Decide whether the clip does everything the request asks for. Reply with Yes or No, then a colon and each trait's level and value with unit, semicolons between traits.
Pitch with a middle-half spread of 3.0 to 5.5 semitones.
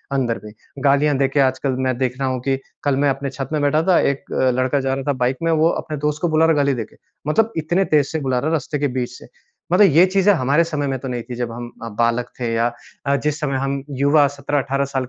No: narrow, 2.6 semitones